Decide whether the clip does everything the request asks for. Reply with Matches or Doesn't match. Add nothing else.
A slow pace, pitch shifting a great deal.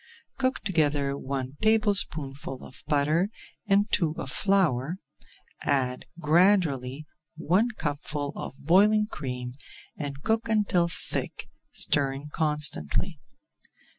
Matches